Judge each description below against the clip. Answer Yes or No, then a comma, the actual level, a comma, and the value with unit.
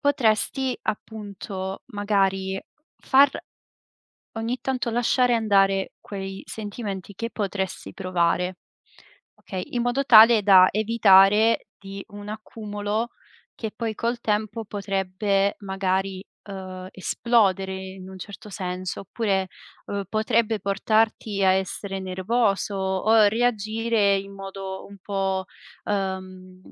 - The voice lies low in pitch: No, high, 200 Hz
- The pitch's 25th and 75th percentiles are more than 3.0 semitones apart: No, narrow, 2.5 semitones